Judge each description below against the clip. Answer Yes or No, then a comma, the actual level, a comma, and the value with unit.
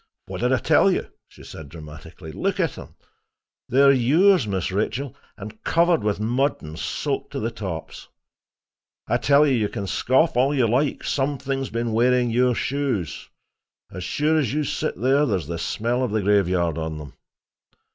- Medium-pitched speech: No, low, 115 Hz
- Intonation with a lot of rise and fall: Yes, wide, 6.5 semitones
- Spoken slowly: No, average, 175 wpm